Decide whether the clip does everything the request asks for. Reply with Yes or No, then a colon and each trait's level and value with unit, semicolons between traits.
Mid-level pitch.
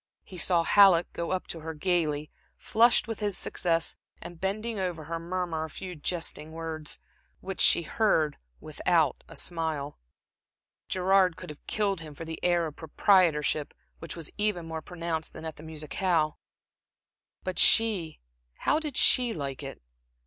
Yes: medium, 170 Hz